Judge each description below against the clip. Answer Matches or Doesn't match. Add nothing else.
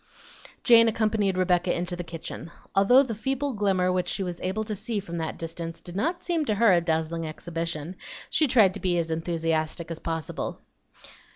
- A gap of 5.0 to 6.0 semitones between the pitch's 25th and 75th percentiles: Doesn't match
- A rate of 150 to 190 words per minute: Matches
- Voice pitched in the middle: Matches